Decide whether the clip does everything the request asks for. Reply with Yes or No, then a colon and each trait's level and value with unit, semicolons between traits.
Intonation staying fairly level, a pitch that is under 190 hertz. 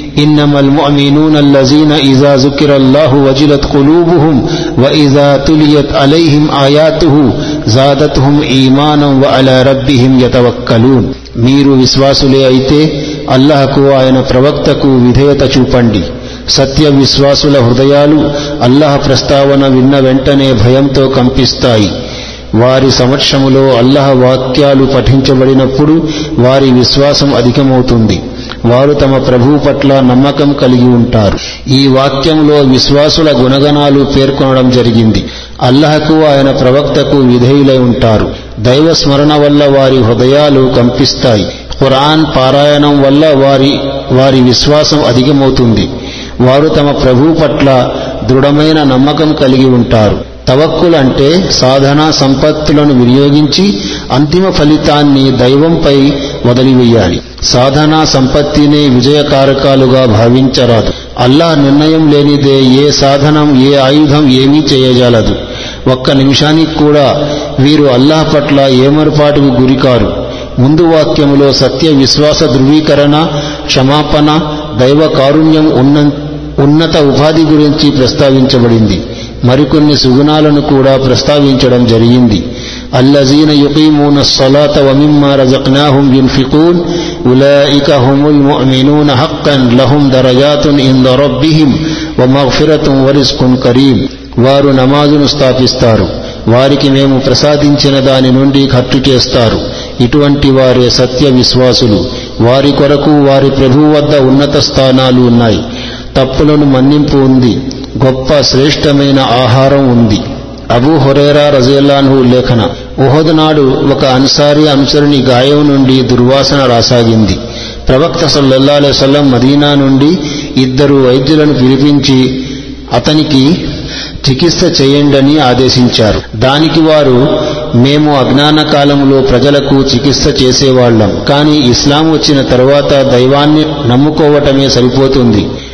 Yes: narrow, 2.2 semitones; medium, 140 Hz